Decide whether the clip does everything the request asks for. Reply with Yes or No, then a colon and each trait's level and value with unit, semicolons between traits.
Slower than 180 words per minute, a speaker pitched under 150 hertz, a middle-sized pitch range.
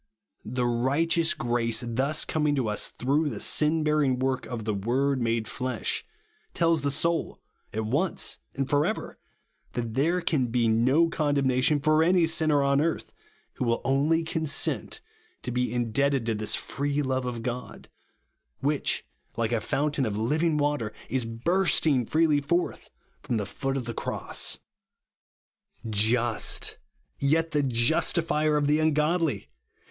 Yes: average, 150 wpm; medium, 140 Hz; average, 4.3 semitones